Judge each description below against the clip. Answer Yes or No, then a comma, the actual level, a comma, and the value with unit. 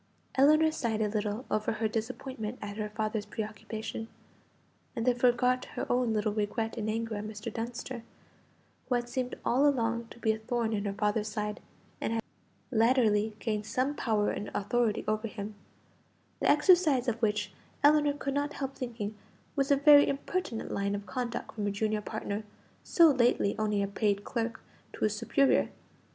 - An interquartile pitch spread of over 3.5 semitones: No, average, 3.1 semitones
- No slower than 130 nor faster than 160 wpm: No, average, 170 wpm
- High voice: Yes, high, 225 Hz